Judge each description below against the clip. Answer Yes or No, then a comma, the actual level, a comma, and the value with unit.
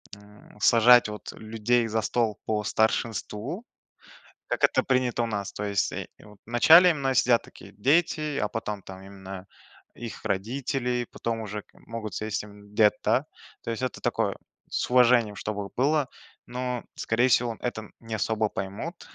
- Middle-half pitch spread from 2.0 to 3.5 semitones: Yes, average, 2.9 semitones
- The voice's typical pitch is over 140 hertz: No, low, 115 Hz